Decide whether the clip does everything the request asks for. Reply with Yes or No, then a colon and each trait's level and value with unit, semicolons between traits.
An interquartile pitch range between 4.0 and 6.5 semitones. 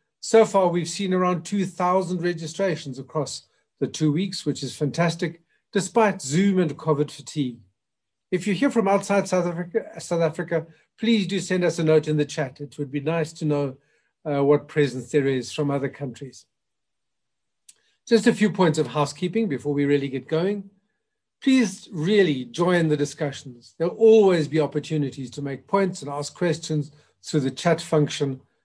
Yes: average, 4.3 semitones